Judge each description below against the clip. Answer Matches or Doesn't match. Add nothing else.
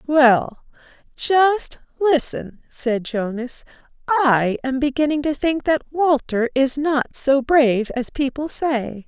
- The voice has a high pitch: Matches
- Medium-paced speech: Doesn't match